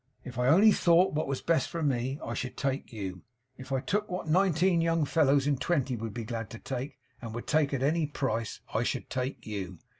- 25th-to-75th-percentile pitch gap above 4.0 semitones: Yes, average, 5.0 semitones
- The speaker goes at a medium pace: No, fast, 220 wpm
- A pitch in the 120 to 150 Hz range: Yes, low, 135 Hz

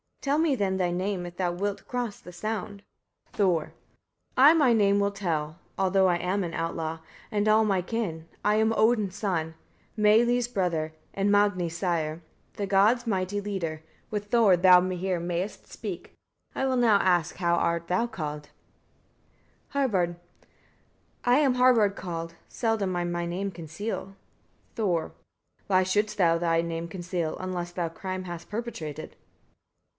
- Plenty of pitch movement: No, average, 3.6 semitones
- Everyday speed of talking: Yes, average, 155 wpm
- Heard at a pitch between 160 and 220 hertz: Yes, medium, 185 Hz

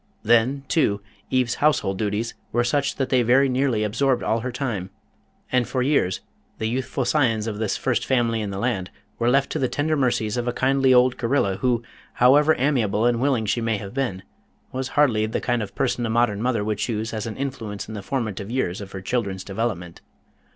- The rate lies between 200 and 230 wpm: Yes, fast, 205 wpm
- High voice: No, low, 120 Hz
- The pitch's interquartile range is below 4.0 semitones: Yes, average, 3.5 semitones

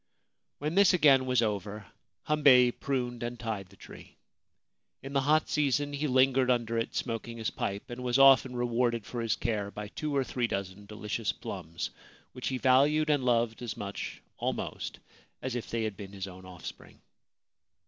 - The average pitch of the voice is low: Yes, low, 120 Hz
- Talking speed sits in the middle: Yes, average, 175 wpm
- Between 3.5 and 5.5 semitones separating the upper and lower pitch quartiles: Yes, average, 4.1 semitones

